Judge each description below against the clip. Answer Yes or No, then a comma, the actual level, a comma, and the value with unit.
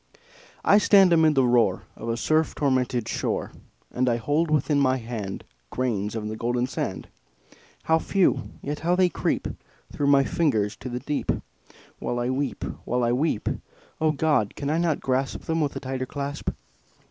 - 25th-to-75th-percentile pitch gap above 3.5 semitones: Yes, average, 4.2 semitones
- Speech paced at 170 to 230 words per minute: Yes, average, 175 wpm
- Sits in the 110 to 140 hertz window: Yes, low, 135 Hz